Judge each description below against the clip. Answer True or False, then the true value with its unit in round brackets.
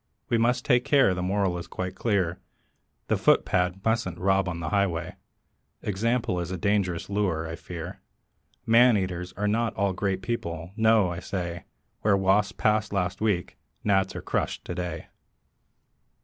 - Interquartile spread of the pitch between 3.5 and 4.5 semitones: False (3.0 semitones)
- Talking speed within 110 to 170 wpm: True (160 wpm)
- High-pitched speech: False (95 Hz)